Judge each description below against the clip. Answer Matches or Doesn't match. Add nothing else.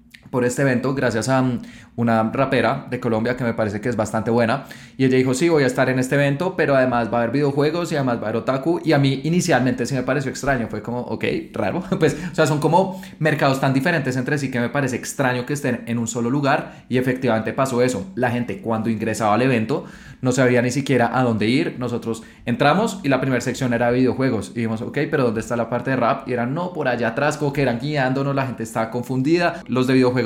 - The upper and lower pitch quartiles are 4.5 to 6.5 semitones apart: Doesn't match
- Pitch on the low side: Matches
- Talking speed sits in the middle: Doesn't match